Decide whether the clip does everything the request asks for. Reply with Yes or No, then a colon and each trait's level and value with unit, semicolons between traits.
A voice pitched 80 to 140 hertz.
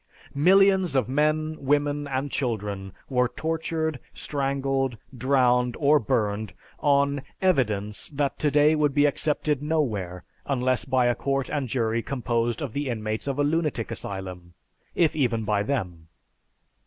Yes: low, 135 Hz